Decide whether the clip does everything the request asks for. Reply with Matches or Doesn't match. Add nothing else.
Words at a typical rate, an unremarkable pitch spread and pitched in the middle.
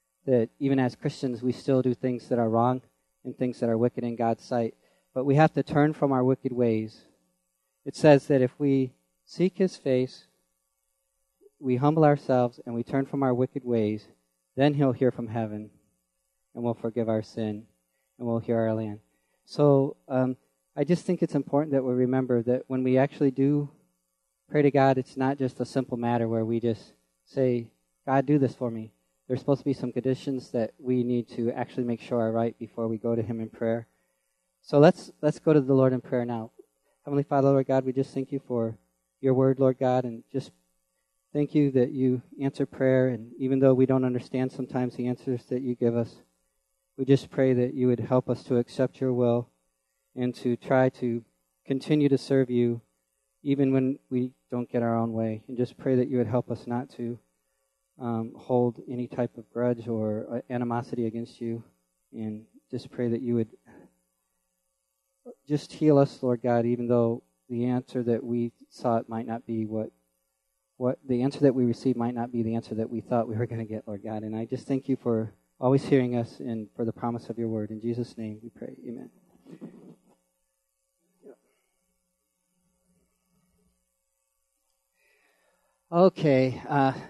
Doesn't match